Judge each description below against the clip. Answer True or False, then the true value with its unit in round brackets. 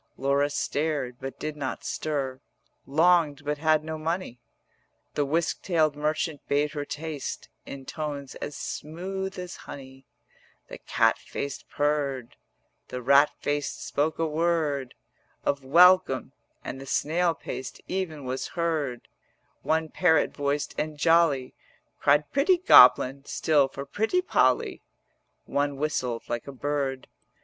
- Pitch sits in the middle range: True (145 Hz)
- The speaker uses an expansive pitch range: False (2.7 semitones)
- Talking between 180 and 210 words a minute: False (135 wpm)